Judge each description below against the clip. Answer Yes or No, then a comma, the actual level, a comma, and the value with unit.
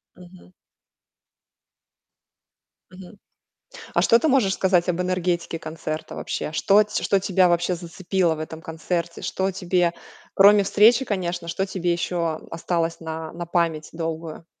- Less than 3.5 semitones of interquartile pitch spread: Yes, narrow, 2.4 semitones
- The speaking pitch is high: No, medium, 175 Hz